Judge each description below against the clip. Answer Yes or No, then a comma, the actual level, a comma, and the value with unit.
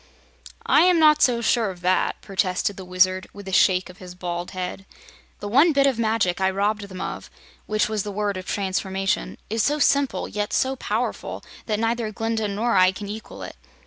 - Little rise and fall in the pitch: No, average, 3.4 semitones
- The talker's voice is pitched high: Yes, high, 205 Hz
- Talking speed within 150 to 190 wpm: No, average, 200 wpm